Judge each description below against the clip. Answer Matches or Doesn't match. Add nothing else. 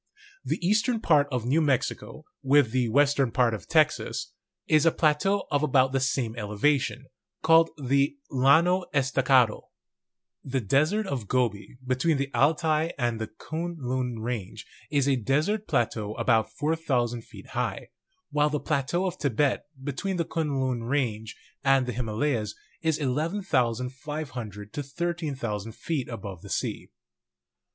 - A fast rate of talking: Doesn't match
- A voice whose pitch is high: Doesn't match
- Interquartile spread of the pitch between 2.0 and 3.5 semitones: Doesn't match